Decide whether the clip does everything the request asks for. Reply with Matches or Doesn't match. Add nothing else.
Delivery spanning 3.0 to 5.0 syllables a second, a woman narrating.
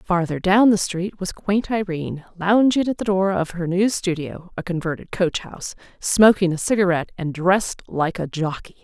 Matches